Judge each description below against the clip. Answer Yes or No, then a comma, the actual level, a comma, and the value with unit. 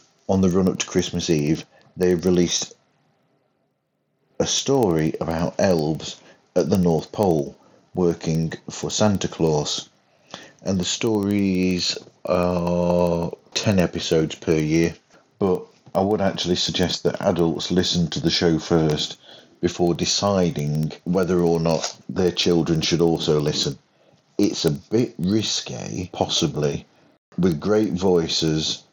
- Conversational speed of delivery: No, slow, 120 wpm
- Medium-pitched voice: No, very low, 85 Hz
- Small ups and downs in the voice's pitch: Yes, narrow, 1.9 semitones